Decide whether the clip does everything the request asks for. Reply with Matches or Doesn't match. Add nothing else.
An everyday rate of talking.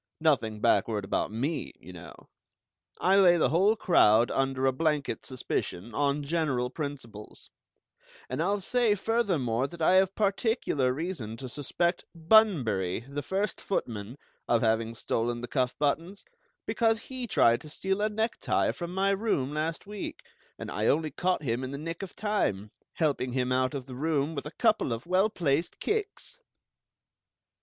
Matches